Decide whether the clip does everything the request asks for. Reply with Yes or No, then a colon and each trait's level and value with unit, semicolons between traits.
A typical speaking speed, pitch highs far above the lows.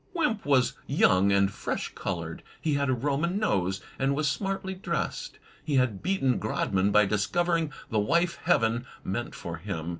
Yes: average, 160 wpm; wide, 8.8 semitones